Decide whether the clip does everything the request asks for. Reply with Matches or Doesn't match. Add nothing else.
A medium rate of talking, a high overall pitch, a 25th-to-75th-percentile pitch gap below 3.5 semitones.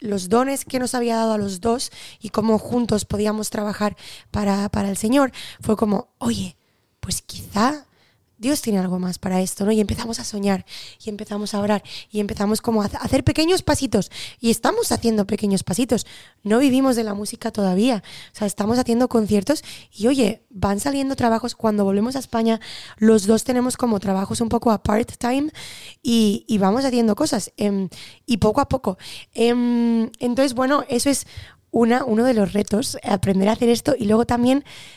Matches